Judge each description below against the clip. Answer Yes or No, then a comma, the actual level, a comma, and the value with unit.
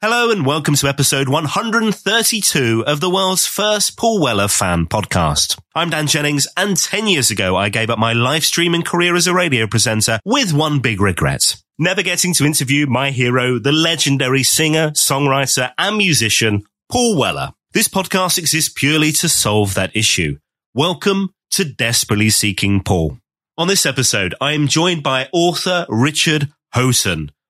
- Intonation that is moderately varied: No, wide, 7.4 semitones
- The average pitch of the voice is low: No, medium, 145 Hz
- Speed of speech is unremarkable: Yes, average, 160 wpm